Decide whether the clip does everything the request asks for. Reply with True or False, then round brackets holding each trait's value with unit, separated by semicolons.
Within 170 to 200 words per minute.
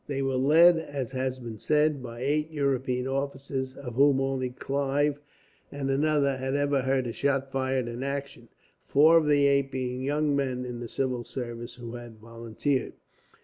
True (175 wpm)